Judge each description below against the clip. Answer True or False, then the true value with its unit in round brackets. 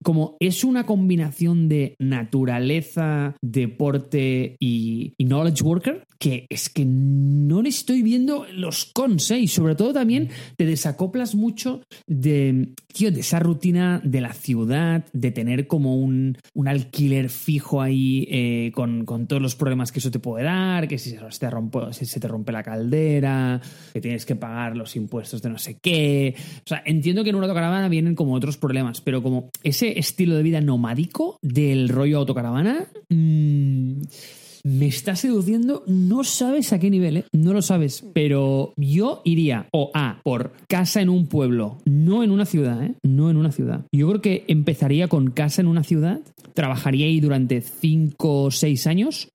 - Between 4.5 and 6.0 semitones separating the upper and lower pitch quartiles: True (5.0 semitones)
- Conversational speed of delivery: True (180 wpm)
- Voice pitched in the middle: True (150 Hz)